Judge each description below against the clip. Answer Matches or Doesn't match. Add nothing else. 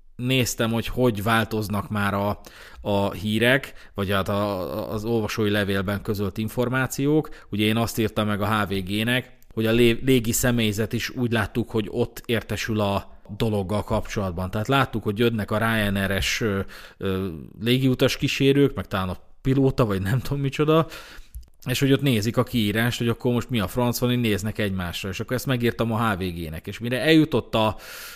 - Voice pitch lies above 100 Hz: Matches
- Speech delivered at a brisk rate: Matches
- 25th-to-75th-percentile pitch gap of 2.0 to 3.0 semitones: Doesn't match